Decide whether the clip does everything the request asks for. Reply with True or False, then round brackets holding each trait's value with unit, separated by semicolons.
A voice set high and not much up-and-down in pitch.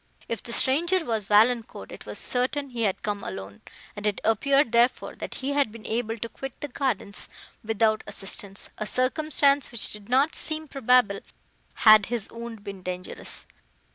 False (230 Hz; 4.2 semitones)